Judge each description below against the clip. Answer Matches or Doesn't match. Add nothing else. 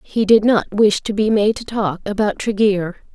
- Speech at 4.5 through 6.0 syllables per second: Matches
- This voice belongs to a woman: Matches